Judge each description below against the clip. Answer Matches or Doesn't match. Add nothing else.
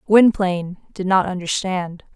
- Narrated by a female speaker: Matches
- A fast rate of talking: Doesn't match